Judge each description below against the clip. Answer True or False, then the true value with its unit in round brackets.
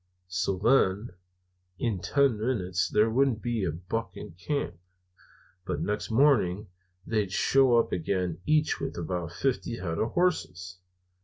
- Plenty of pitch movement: True (5.7 semitones)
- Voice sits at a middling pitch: False (105 Hz)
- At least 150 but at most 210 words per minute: False (140 wpm)